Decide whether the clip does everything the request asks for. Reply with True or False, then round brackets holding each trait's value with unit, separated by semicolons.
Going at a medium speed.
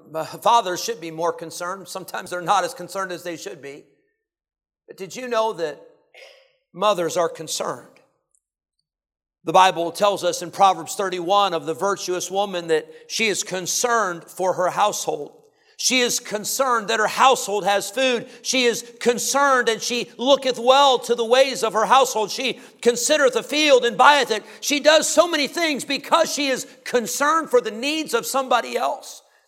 True (170 wpm)